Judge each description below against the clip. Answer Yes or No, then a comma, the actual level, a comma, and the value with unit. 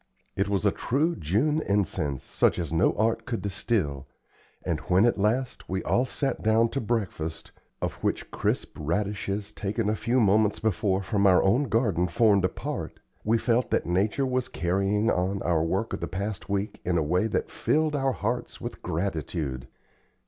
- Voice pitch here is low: Yes, low, 100 Hz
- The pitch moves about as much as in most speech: Yes, average, 4.1 semitones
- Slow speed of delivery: No, average, 180 wpm